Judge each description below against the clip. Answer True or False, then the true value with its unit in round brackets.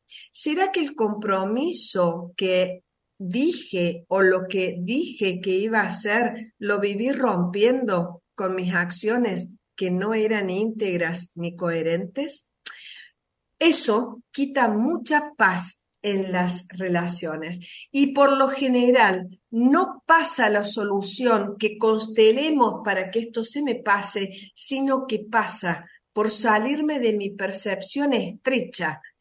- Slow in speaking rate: True (120 wpm)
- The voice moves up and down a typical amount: True (4.9 semitones)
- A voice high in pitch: True (215 Hz)